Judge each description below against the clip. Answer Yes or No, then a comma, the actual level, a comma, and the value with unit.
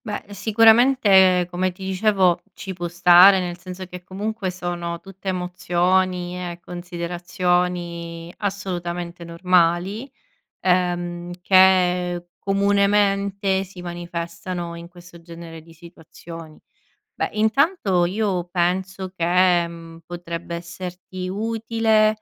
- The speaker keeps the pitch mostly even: Yes, narrow, 1.9 semitones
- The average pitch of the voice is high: No, medium, 180 Hz